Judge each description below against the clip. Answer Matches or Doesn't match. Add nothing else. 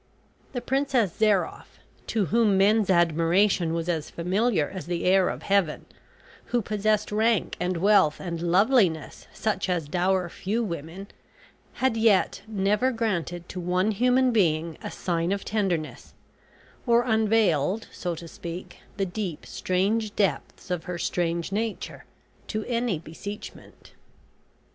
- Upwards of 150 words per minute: Doesn't match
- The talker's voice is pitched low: Doesn't match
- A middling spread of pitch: Matches